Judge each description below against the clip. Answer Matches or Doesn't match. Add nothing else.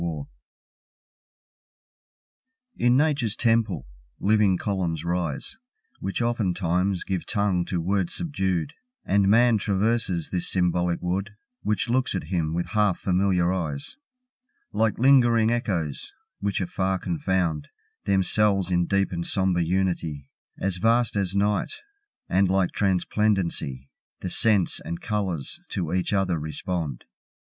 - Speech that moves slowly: Matches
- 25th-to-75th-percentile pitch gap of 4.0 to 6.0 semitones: Doesn't match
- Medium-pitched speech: Doesn't match